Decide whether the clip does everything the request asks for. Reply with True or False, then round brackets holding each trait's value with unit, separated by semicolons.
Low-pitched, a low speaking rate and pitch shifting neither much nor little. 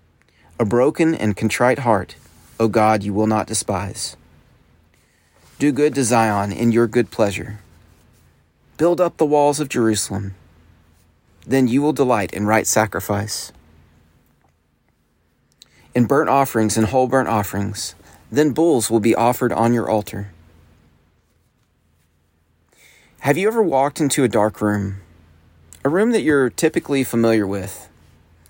False (110 Hz; 130 wpm; 7.3 semitones)